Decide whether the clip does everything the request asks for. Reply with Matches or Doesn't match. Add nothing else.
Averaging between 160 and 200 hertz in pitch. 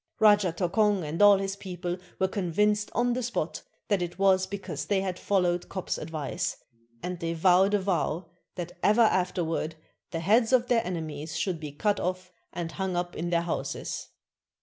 Matches